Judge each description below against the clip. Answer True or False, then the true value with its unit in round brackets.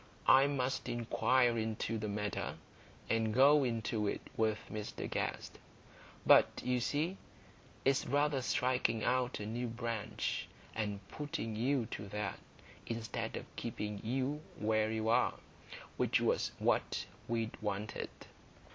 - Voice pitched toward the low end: True (115 Hz)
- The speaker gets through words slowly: True (130 wpm)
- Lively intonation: False (3.1 semitones)